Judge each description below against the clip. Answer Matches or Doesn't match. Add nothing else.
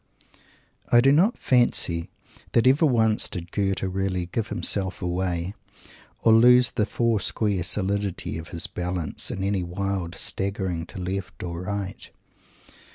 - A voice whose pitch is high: Doesn't match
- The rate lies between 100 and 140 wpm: Matches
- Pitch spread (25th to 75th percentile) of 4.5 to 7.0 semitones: Doesn't match